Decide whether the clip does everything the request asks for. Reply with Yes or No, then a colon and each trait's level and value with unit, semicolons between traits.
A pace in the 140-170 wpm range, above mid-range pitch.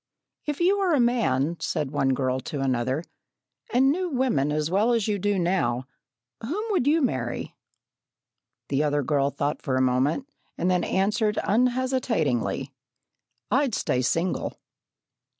No: average, 145 wpm; medium, 175 Hz